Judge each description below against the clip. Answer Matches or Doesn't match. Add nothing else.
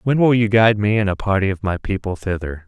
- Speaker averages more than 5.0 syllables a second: Matches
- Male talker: Matches